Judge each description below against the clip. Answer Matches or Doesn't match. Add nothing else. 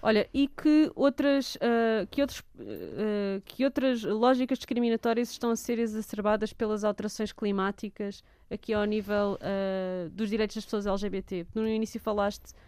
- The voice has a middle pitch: Doesn't match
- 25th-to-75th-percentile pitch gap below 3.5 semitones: Matches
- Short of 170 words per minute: Matches